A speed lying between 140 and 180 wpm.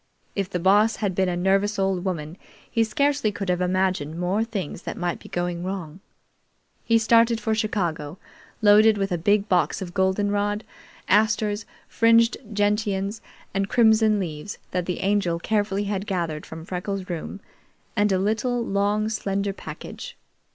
Yes: average, 155 wpm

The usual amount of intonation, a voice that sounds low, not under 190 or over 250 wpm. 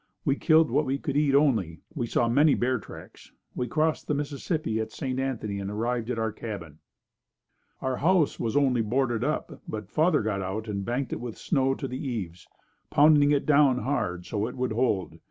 Yes: average, 4.7 semitones; low, 125 Hz; average, 195 wpm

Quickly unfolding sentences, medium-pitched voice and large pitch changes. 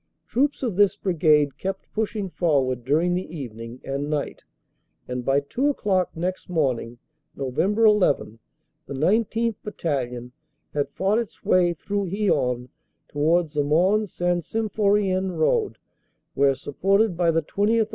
No: average, 140 wpm; medium, 175 Hz; wide, 6.4 semitones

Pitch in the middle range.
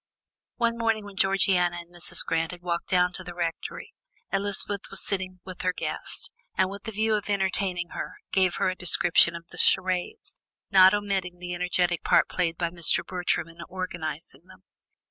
Yes: medium, 180 Hz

